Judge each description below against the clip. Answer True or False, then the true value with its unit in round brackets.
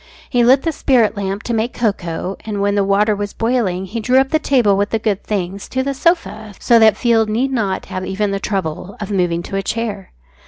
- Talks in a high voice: True (210 Hz)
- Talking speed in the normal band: False (230 wpm)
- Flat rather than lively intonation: False (3.3 semitones)